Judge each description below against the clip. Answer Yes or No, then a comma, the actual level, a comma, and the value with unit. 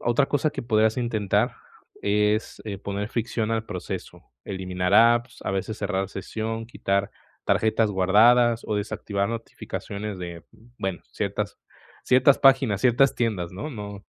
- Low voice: Yes, low, 110 Hz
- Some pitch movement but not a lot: Yes, average, 3.1 semitones